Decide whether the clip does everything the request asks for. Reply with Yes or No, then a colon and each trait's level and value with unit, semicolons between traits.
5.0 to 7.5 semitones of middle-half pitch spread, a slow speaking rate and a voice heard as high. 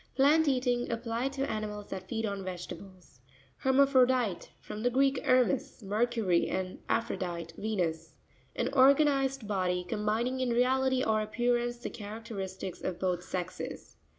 Yes: average, 5.3 semitones; slow, 130 wpm; high, 225 Hz